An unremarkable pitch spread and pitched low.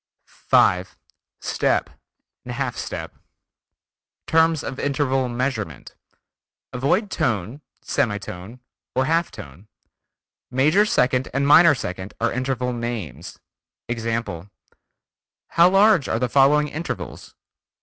Yes: average, 4.4 semitones; low, 125 Hz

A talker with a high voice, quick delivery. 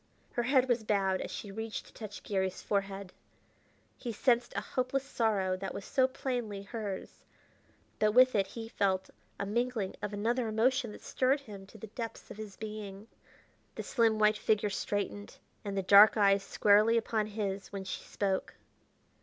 No: high, 210 Hz; average, 170 wpm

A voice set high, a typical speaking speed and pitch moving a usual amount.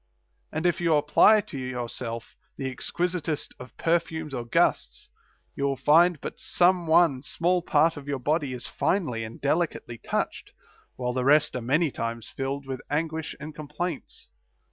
No: medium, 150 Hz; average, 165 wpm; average, 4.3 semitones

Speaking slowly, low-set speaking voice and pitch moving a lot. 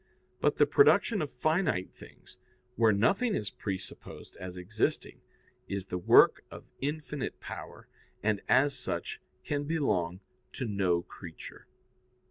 Yes: slow, 125 wpm; low, 110 Hz; wide, 8.0 semitones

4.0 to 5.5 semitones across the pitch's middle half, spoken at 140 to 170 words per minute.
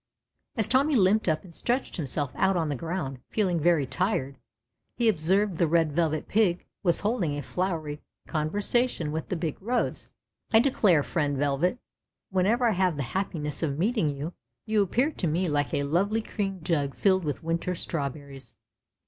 Yes: average, 5.2 semitones; average, 165 wpm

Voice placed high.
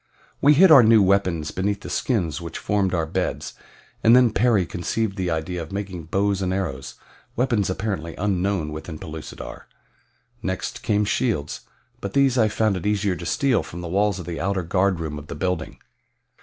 No: very low, 95 Hz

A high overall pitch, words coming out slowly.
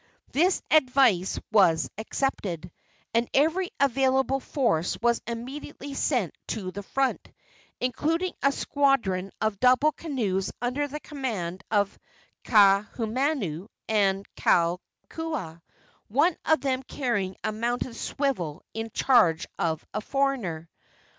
Yes: high, 235 Hz; slow, 110 wpm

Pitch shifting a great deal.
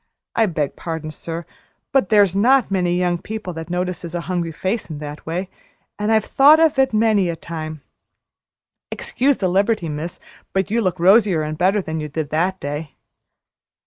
No: average, 4.4 semitones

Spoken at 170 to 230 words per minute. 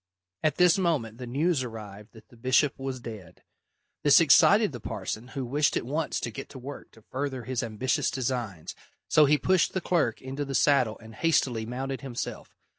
Yes: average, 190 wpm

